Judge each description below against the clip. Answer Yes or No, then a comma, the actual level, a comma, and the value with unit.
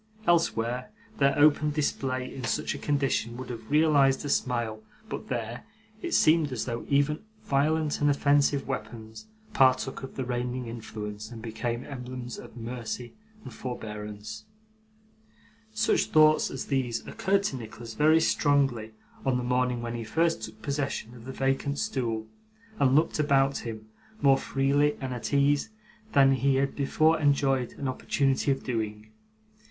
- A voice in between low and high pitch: No, low, 130 Hz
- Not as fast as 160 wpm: Yes, average, 150 wpm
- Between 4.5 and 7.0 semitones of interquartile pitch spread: No, average, 3.4 semitones